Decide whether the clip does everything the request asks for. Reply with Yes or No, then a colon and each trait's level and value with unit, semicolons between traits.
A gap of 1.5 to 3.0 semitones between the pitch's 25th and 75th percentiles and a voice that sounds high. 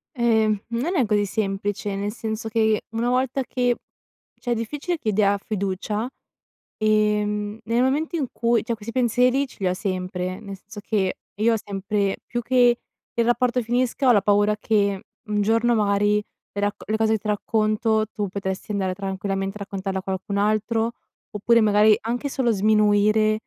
Yes: narrow, 2.5 semitones; high, 215 Hz